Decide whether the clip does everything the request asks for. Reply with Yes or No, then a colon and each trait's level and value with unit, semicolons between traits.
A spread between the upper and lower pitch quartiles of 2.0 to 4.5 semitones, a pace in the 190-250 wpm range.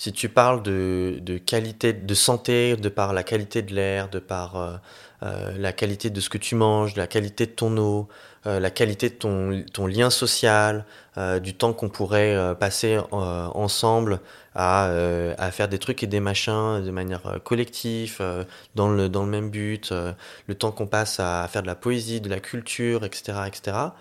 Yes: average, 3.0 semitones; average, 205 wpm